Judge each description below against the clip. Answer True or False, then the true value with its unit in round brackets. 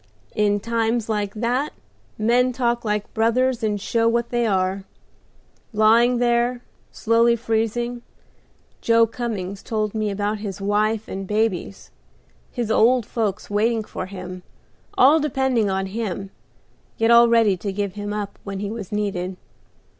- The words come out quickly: False (140 wpm)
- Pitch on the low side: False (220 Hz)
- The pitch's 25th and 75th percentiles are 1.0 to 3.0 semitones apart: True (2.5 semitones)